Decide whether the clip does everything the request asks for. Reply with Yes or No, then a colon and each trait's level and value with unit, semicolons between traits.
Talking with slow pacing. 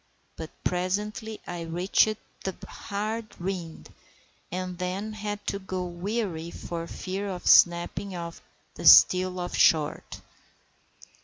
Yes: slow, 110 wpm